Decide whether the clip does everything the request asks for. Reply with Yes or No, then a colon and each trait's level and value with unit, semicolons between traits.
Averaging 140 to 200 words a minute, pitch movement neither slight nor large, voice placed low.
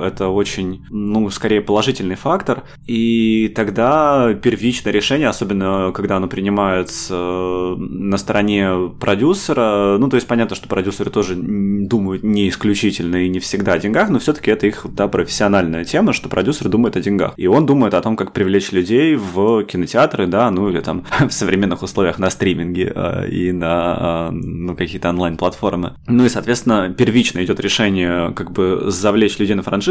Yes: fast, 160 wpm; average, 3.1 semitones; low, 100 Hz